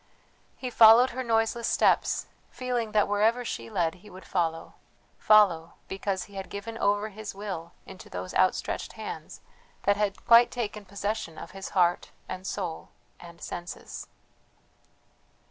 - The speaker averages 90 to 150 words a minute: Yes, average, 145 wpm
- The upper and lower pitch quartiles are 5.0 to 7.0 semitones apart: No, average, 3.6 semitones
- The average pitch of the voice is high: Yes, high, 200 Hz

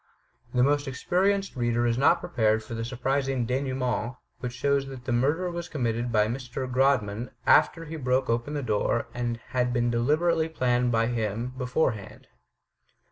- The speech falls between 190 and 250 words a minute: No, average, 175 wpm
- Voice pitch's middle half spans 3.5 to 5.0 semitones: No, average, 2.9 semitones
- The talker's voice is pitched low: Yes, low, 125 Hz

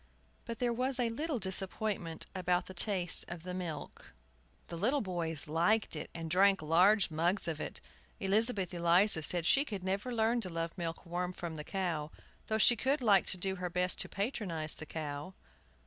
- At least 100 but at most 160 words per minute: No, average, 185 wpm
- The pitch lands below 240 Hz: Yes, medium, 185 Hz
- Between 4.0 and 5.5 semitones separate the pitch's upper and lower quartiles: Yes, average, 4.3 semitones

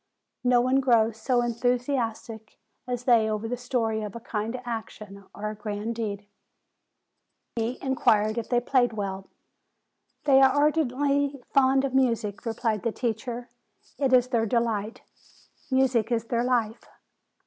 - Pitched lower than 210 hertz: No, high, 235 Hz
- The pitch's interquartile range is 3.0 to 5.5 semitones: No, narrow, 2.6 semitones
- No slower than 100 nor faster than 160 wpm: Yes, average, 140 wpm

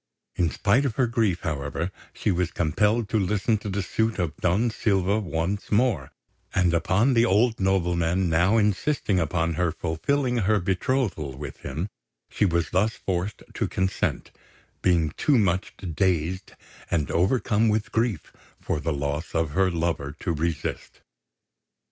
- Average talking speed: Yes, average, 150 wpm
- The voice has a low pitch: Yes, very low, 95 Hz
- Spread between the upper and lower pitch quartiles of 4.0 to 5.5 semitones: Yes, average, 4.3 semitones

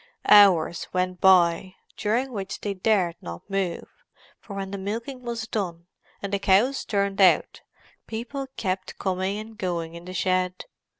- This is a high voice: Yes, high, 195 Hz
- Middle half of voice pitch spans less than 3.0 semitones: Yes, narrow, 2.6 semitones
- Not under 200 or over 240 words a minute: No, average, 155 wpm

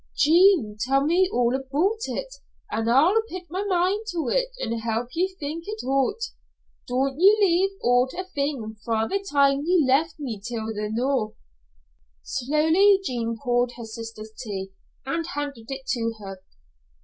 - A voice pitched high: Yes, very high, 275 Hz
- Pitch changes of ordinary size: No, wide, 7.4 semitones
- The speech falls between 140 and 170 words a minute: Yes, average, 160 wpm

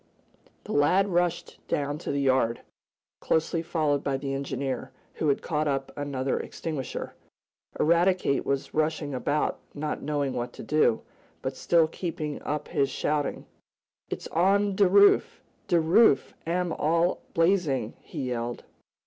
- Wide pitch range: No, average, 3.6 semitones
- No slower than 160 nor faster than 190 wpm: No, average, 140 wpm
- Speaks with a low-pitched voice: No, medium, 150 Hz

